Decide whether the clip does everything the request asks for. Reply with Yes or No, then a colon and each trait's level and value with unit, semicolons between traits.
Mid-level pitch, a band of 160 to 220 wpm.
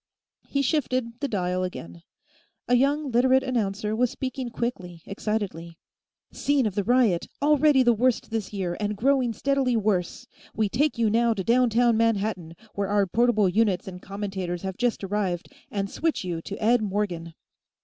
No: high, 215 Hz; average, 165 wpm